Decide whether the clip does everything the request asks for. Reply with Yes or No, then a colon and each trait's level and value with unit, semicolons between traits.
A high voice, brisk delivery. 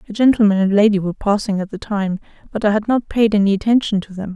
Yes: high, 205 Hz; fast, 250 wpm